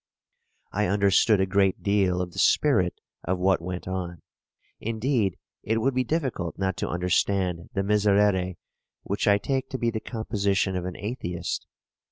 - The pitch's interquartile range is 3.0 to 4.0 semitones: Yes, average, 3.3 semitones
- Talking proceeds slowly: No, average, 160 wpm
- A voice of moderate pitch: No, low, 100 Hz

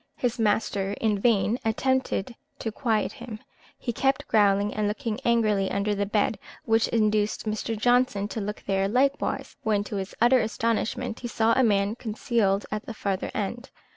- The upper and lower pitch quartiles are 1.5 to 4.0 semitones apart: Yes, narrow, 2.5 semitones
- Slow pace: No, average, 170 wpm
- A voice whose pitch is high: Yes, high, 215 Hz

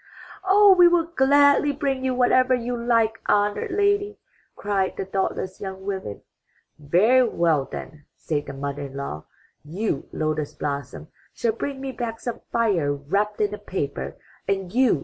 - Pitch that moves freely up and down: Yes, wide, 9.0 semitones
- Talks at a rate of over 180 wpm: No, average, 160 wpm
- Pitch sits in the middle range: No, high, 210 Hz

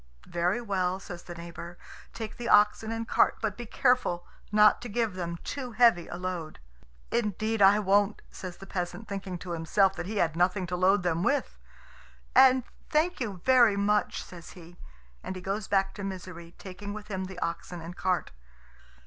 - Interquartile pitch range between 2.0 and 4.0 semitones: Yes, average, 3.2 semitones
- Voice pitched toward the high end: Yes, high, 195 Hz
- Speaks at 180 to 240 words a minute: Yes, average, 185 wpm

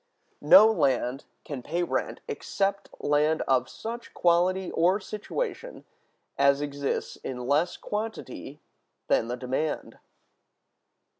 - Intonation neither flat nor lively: No, wide, 6.3 semitones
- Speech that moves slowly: Yes, slow, 105 wpm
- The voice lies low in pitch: No, medium, 155 Hz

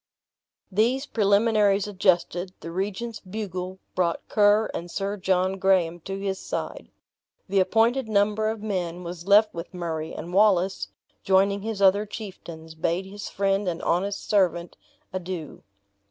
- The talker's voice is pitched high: Yes, high, 195 Hz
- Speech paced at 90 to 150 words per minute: Yes, average, 140 wpm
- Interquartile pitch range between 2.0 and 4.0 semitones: Yes, narrow, 2.5 semitones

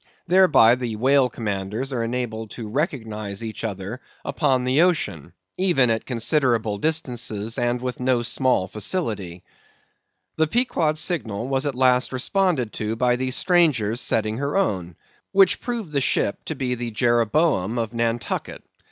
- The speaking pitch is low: Yes, low, 125 Hz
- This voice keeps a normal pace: Yes, average, 145 wpm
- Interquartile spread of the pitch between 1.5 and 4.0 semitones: No, average, 4.5 semitones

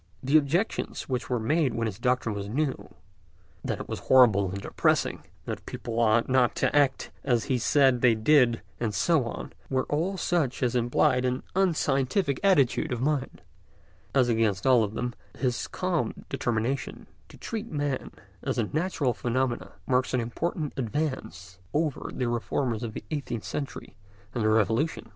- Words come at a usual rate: Yes, average, 160 wpm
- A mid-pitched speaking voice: No, low, 125 Hz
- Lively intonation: No, average, 3.9 semitones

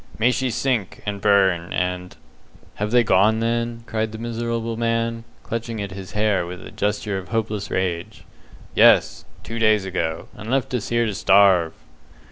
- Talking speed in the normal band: Yes, average, 170 wpm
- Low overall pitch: Yes, low, 110 Hz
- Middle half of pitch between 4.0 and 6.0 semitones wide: No, average, 3.2 semitones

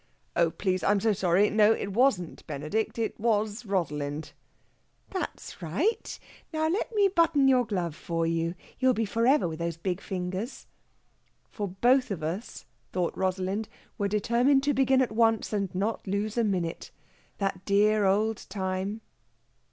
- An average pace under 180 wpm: Yes, average, 155 wpm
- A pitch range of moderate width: Yes, average, 4.3 semitones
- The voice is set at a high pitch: Yes, high, 205 Hz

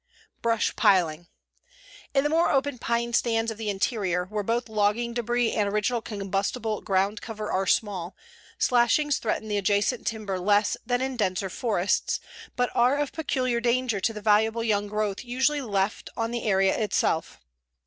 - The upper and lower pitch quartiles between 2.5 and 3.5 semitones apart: Yes, average, 3.0 semitones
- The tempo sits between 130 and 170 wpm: Yes, average, 160 wpm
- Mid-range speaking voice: No, high, 220 Hz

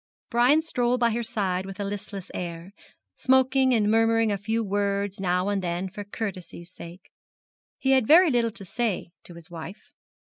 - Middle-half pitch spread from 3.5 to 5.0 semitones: Yes, average, 4.1 semitones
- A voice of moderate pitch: No, high, 205 Hz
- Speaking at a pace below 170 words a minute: No, average, 175 wpm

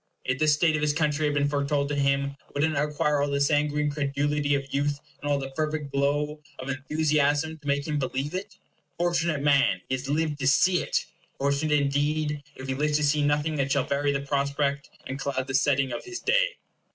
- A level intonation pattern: Yes, narrow, 1.3 semitones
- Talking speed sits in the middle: No, fast, 215 wpm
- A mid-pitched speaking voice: Yes, medium, 145 Hz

